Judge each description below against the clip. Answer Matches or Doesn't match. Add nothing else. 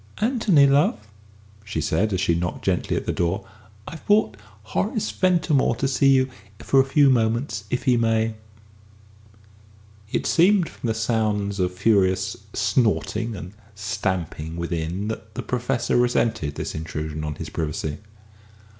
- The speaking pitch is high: Doesn't match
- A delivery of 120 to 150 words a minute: Matches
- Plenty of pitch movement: Matches